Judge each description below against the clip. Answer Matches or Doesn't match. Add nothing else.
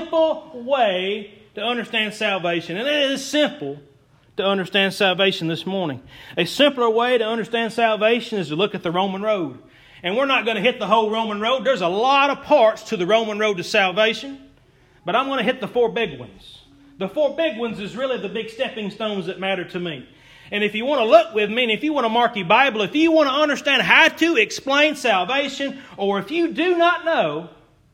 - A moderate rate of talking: Doesn't match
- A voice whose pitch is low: Doesn't match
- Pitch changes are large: Matches